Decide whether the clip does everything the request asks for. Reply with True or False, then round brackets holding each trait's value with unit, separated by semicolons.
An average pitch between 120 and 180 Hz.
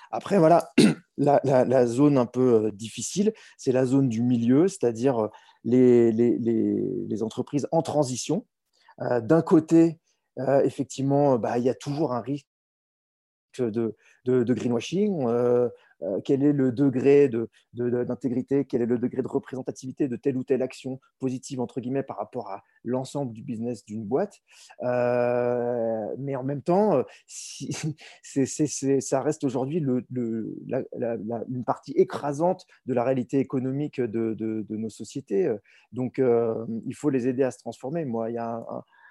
True (130 Hz)